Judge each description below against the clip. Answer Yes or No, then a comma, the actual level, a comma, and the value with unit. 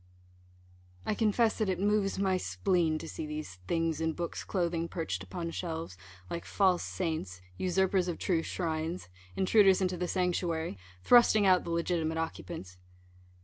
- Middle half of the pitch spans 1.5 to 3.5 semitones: Yes, average, 2.7 semitones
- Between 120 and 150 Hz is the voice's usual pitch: No, medium, 175 Hz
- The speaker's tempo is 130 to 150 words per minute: Yes, average, 145 wpm